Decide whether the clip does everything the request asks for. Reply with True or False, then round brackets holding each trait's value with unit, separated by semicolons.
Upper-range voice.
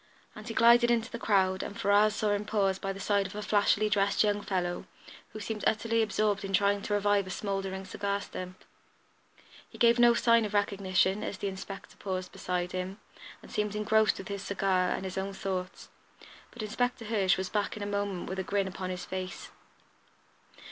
True (200 Hz)